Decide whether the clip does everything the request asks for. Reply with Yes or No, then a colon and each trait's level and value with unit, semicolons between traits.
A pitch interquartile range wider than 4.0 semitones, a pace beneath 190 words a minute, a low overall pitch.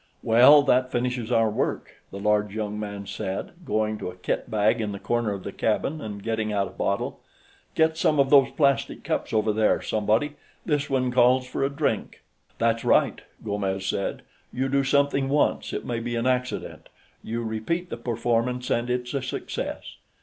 No: average, 3.7 semitones; average, 180 wpm; low, 115 Hz